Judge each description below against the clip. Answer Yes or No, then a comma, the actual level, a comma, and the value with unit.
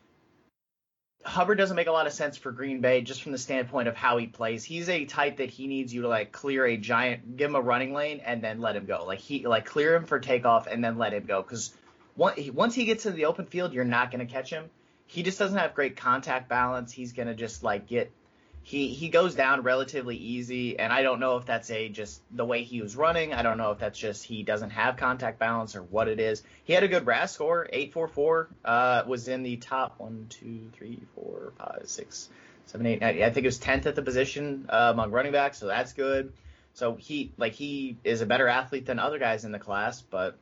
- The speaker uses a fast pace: Yes, fast, 240 wpm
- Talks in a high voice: No, low, 125 Hz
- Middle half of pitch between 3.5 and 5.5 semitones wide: Yes, average, 3.8 semitones